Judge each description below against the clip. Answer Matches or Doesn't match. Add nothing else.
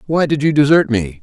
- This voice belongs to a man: Matches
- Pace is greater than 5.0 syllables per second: Matches